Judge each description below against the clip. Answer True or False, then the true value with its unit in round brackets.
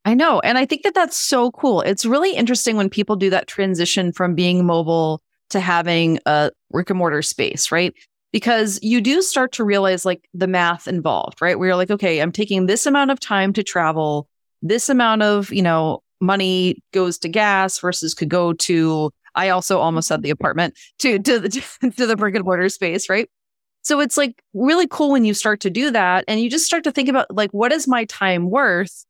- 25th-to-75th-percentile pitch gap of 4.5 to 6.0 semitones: True (5.3 semitones)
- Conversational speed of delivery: False (215 wpm)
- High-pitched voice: True (195 Hz)